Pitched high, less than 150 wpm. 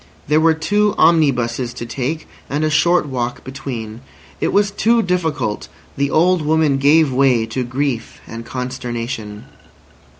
No: medium, 140 Hz; average, 140 wpm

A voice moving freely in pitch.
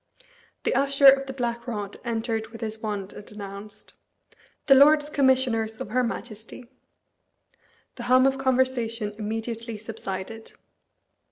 No: average, 3.2 semitones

